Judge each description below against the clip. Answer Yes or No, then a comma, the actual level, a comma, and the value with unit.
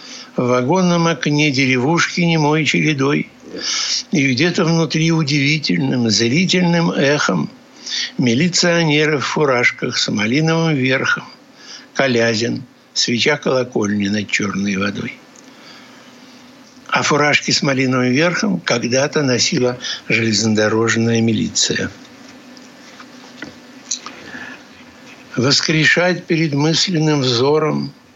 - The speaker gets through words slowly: Yes, slow, 80 wpm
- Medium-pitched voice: Yes, medium, 160 Hz